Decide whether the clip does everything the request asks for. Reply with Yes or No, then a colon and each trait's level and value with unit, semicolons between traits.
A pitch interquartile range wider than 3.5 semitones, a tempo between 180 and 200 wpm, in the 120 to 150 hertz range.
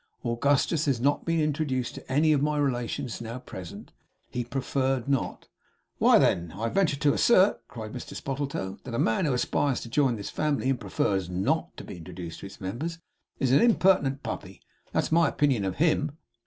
Yes: average, 4.5 semitones; average, 190 wpm; low, 135 Hz